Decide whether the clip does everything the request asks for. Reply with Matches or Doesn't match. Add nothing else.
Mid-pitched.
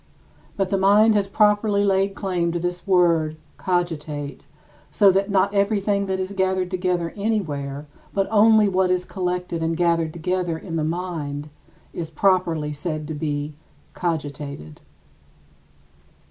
Matches